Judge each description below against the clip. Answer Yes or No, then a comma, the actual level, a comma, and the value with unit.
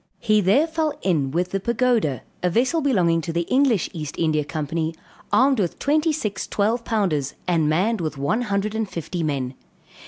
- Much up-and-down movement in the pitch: Yes, wide, 6.7 semitones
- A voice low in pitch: No, high, 190 Hz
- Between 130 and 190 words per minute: Yes, average, 180 wpm